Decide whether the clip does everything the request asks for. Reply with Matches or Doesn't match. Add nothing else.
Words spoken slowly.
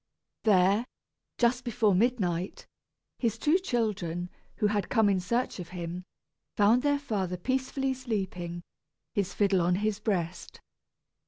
Matches